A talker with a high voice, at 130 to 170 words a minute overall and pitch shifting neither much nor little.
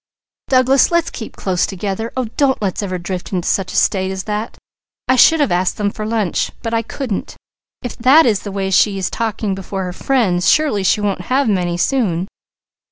No: high, 205 Hz; average, 200 wpm; average, 4.6 semitones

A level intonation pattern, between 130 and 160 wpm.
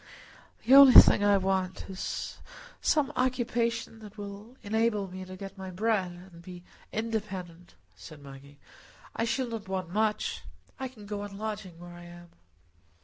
No: average, 3.7 semitones; average, 155 wpm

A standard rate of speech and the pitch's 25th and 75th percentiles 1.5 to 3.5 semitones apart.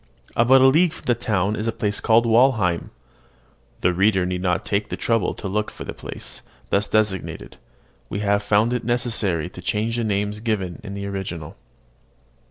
Yes: average, 180 wpm; average, 3.1 semitones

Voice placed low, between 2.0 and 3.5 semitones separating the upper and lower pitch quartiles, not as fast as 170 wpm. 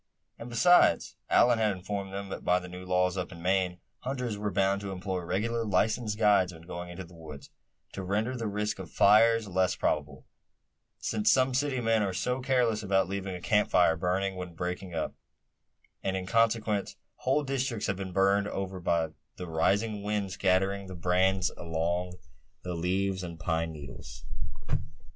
No: very low, 95 Hz; average, 2.9 semitones; average, 175 wpm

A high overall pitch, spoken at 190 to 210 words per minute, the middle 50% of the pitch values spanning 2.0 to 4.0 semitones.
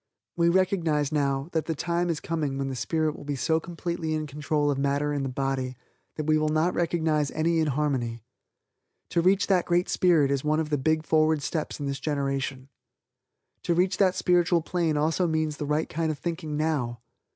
No: medium, 155 Hz; average, 195 wpm; average, 2.9 semitones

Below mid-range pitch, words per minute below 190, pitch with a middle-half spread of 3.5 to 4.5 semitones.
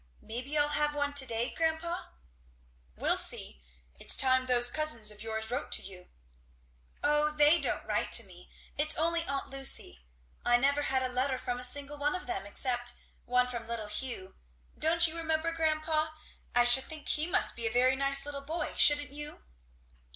No: very high, 275 Hz; average, 180 wpm; average, 4.0 semitones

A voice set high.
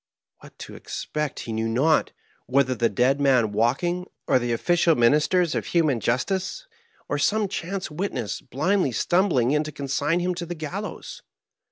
No: medium, 150 Hz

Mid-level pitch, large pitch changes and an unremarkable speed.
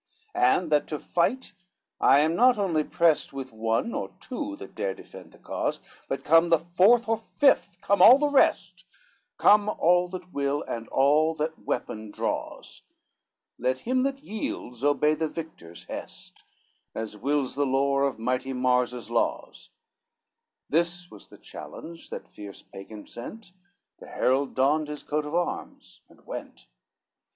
Yes: medium, 155 Hz; wide, 5.8 semitones; average, 160 wpm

